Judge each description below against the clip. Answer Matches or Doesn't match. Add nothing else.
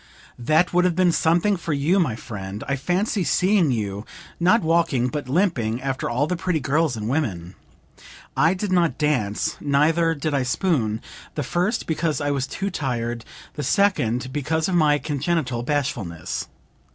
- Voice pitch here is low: Doesn't match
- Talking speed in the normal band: Matches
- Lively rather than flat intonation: Matches